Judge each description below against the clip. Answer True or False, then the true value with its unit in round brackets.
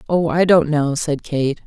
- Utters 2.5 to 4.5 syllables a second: True (4.1 syllables/s)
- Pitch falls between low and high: True (155 Hz)